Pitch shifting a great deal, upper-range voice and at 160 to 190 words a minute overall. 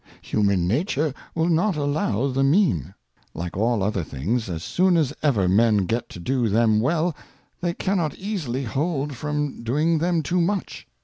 No: wide, 7.3 semitones; low, 135 Hz; average, 170 wpm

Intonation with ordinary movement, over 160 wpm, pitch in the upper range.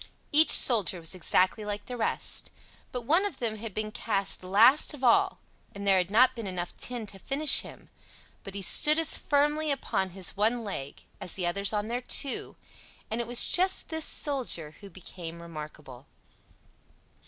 No: wide, 5.7 semitones; average, 175 wpm; high, 215 Hz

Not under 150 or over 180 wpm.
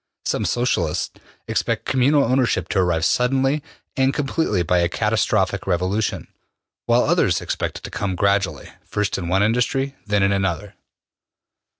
No: average, 140 wpm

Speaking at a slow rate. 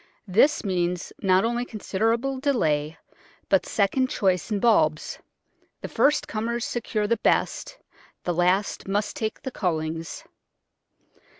Yes: slow, 120 wpm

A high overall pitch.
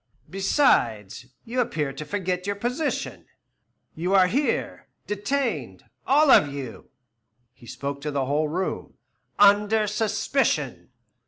Yes: high, 195 Hz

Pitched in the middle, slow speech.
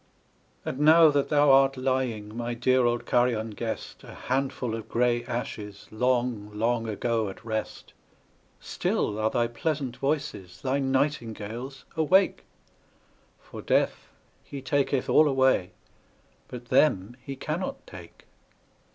No: low, 125 Hz; slow, 125 wpm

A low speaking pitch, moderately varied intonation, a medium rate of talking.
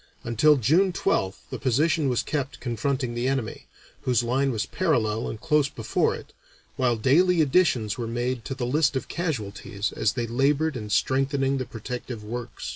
Yes: low, 130 Hz; average, 3.7 semitones; average, 170 wpm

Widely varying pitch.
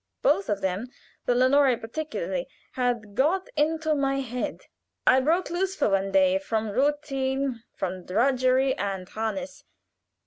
No: average, 4.6 semitones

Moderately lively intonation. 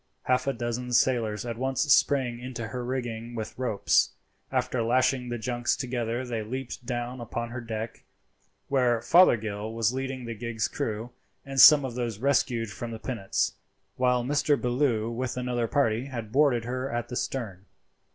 No: narrow, 2.0 semitones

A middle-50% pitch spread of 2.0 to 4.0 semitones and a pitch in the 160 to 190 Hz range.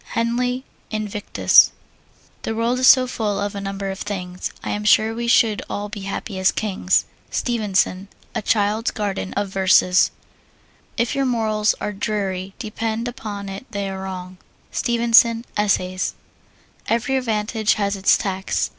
No: average, 2.8 semitones; high, 210 Hz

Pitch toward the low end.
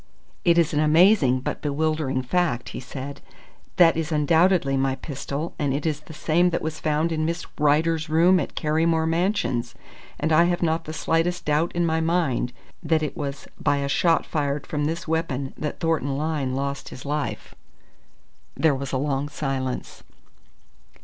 No: medium, 155 Hz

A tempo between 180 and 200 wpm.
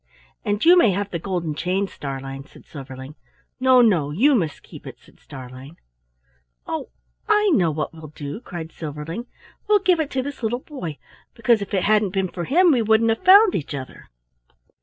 Yes: average, 185 wpm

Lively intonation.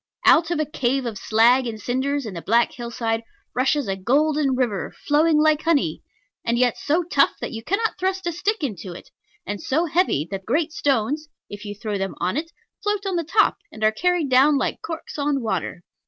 Yes: wide, 5.9 semitones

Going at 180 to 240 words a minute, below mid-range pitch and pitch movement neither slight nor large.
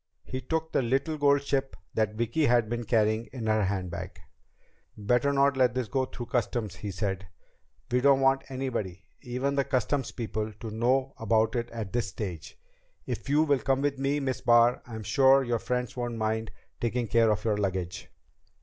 Yes: average, 185 wpm; low, 120 Hz; average, 3.7 semitones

